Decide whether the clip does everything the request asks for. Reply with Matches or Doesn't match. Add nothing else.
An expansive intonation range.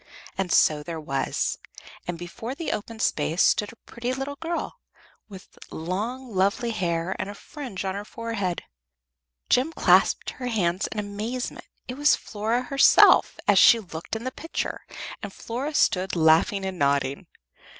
Matches